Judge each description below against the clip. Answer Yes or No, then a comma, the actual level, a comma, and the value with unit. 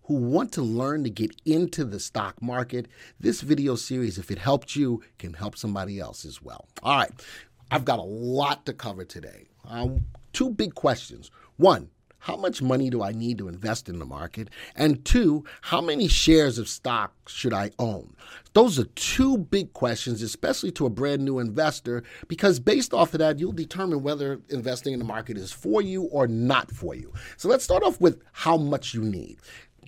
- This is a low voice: Yes, low, 125 Hz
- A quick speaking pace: No, average, 195 wpm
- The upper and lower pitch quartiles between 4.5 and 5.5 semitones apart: Yes, average, 5.1 semitones